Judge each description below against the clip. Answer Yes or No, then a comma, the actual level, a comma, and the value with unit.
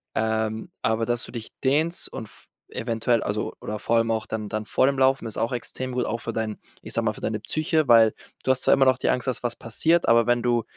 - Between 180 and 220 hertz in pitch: No, low, 115 Hz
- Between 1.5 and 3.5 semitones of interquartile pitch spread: Yes, average, 2.7 semitones